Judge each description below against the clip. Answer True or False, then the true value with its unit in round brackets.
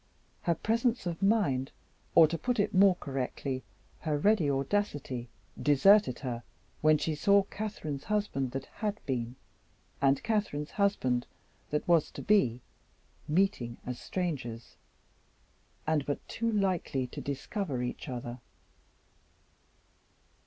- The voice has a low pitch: False (155 Hz)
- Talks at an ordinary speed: False (120 wpm)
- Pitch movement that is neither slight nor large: False (7.3 semitones)